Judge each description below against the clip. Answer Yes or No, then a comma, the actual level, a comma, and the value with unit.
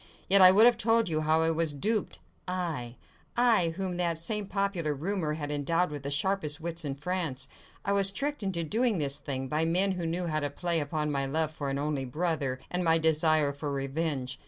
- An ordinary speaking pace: No, fast, 210 wpm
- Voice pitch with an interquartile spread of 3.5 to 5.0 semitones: Yes, average, 4.1 semitones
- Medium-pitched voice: Yes, medium, 160 Hz